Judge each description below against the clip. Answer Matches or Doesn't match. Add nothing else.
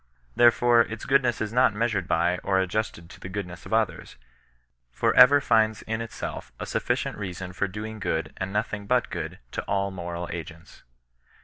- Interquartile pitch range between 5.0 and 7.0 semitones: Doesn't match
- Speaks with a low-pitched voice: Matches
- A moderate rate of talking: Matches